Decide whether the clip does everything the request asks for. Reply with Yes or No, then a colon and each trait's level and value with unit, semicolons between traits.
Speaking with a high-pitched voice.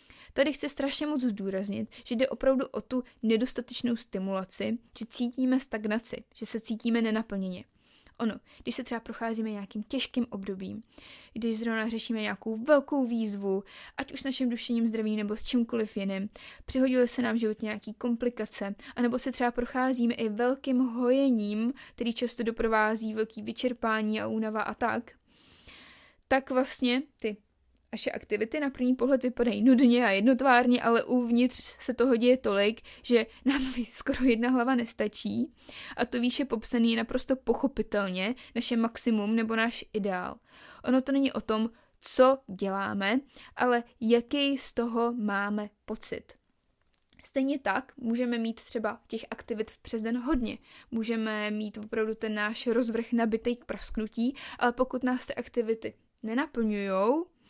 Yes: high, 235 Hz